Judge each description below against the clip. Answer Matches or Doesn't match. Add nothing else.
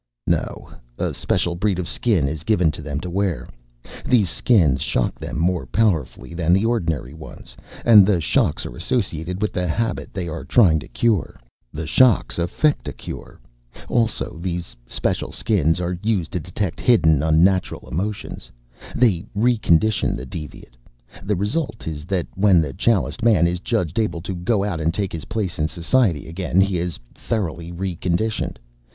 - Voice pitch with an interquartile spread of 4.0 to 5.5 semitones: Matches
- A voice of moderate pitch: Doesn't match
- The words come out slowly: Doesn't match